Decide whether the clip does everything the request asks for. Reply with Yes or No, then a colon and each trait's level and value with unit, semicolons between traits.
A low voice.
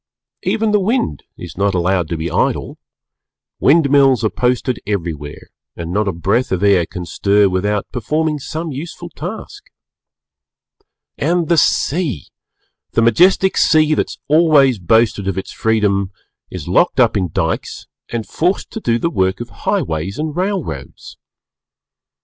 Yes: low, 115 Hz